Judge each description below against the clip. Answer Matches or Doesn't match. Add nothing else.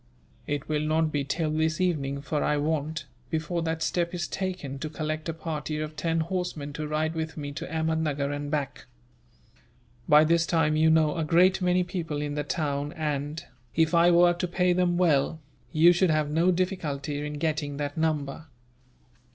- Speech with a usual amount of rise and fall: Doesn't match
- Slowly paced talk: Doesn't match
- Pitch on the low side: Doesn't match